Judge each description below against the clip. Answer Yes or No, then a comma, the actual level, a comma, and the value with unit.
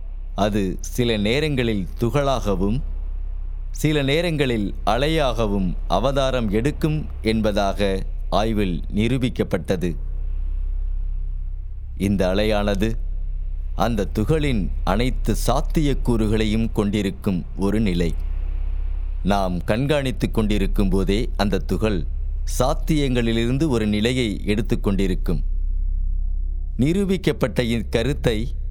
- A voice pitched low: Yes, low, 100 Hz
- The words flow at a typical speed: No, slow, 70 wpm